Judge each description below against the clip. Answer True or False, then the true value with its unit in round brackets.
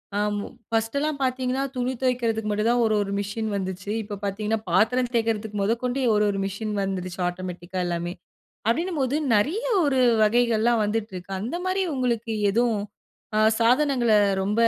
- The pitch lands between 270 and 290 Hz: False (225 Hz)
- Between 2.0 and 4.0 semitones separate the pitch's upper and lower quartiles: True (3.7 semitones)